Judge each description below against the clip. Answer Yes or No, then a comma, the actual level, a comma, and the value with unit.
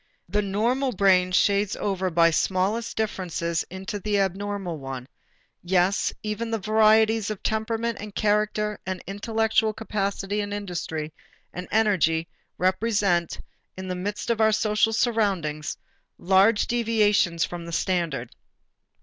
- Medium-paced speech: No, slow, 125 wpm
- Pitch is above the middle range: Yes, high, 200 Hz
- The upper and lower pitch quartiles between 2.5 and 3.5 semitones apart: Yes, average, 3.1 semitones